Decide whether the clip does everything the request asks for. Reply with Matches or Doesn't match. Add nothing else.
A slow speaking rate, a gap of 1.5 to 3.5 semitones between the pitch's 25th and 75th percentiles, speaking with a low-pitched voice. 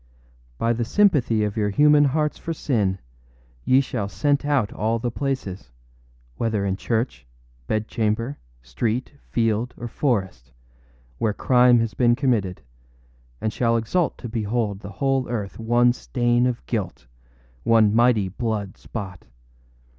Doesn't match